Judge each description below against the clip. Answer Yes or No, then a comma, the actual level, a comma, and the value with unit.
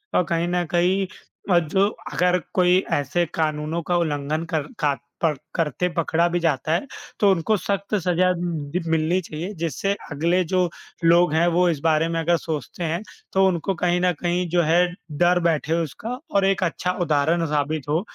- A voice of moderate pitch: Yes, medium, 170 Hz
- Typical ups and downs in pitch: No, narrow, 2.3 semitones